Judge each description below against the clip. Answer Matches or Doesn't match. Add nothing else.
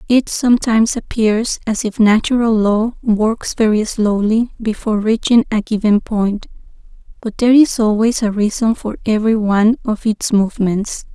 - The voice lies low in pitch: Doesn't match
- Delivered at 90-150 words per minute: Matches